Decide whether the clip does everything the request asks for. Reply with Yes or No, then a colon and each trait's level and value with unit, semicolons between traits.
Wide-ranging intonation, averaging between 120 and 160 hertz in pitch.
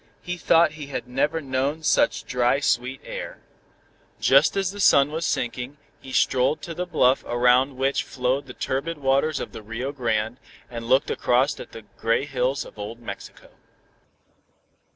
No: average, 3.0 semitones; low, 135 Hz